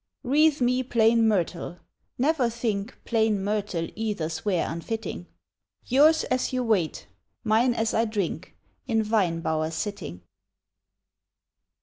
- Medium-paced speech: No, slow, 115 wpm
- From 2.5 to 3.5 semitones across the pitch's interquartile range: No, average, 5.3 semitones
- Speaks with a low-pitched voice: No, high, 220 Hz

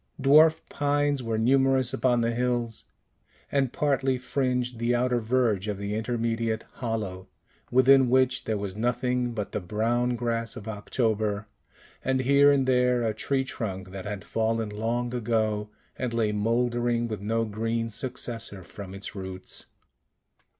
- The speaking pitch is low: Yes, low, 115 Hz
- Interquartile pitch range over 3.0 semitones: No, average, 2.7 semitones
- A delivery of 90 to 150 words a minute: Yes, average, 145 wpm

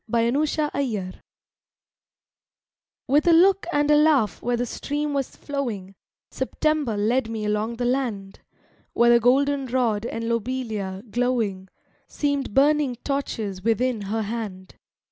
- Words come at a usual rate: No, slow, 130 wpm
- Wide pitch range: No, average, 4.8 semitones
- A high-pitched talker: Yes, high, 240 Hz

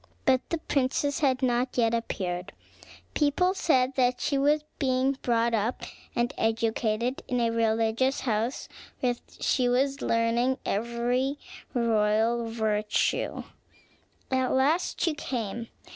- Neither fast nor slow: No, slow, 120 wpm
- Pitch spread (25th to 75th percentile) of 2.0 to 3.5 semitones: Yes, narrow, 2.6 semitones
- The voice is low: No, high, 245 Hz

